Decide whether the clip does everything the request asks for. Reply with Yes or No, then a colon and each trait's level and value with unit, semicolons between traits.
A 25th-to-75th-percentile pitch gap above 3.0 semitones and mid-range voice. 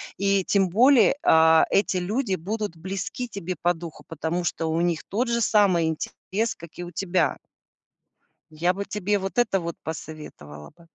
Yes: average, 3.7 semitones; medium, 180 Hz